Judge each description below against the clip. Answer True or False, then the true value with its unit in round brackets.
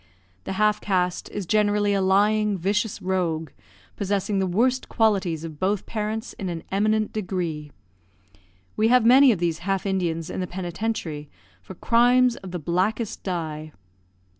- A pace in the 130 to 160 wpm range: True (150 wpm)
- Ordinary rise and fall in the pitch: True (3.6 semitones)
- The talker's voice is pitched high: True (195 Hz)